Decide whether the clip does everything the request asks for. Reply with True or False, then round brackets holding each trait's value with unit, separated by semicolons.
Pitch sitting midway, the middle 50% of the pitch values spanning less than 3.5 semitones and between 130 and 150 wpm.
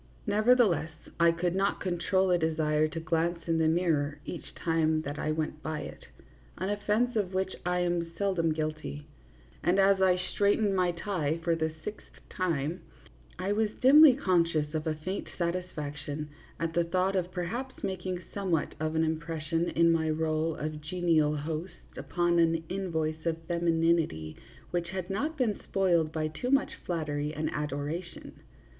False (170 Hz; 3.0 semitones; 165 wpm)